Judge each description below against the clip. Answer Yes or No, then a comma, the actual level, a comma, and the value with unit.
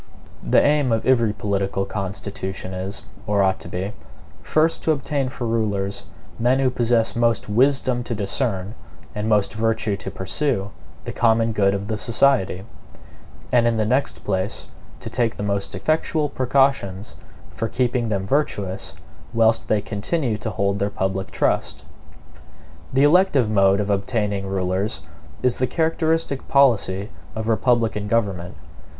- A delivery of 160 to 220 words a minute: No, average, 145 wpm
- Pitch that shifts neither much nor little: Yes, average, 4.3 semitones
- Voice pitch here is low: Yes, low, 110 Hz